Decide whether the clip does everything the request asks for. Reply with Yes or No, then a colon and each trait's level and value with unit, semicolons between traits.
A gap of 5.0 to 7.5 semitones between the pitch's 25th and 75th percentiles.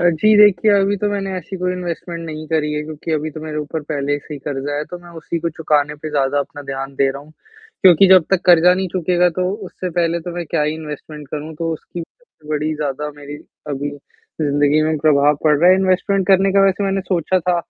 No: average, 3.5 semitones